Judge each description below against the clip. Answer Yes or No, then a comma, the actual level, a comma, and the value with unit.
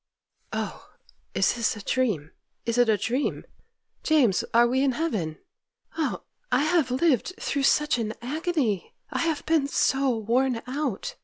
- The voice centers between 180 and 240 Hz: No, very high, 255 Hz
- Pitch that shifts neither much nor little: Yes, average, 4.7 semitones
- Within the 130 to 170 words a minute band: Yes, average, 140 wpm